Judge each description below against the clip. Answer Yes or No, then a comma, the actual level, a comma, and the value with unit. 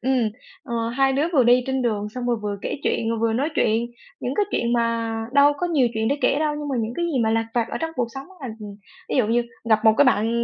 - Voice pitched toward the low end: No, high, 240 Hz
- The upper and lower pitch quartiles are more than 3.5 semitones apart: No, average, 3.2 semitones